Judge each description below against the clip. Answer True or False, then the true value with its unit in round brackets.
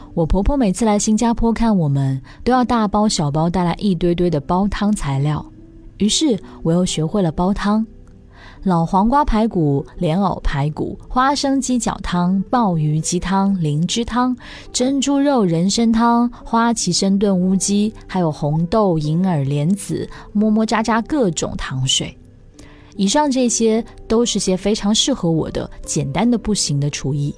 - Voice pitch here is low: False (195 Hz)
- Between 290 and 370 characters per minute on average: False (235 characters per minute)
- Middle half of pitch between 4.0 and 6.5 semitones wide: True (5.5 semitones)